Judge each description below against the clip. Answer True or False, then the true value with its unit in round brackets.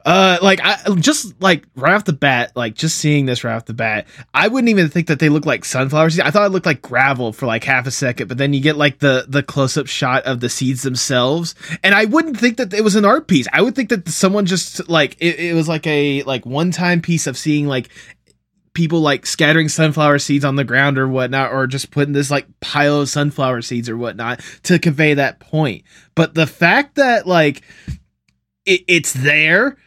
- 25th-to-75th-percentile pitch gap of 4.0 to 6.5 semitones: True (4.4 semitones)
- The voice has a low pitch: False (150 Hz)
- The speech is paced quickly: True (225 wpm)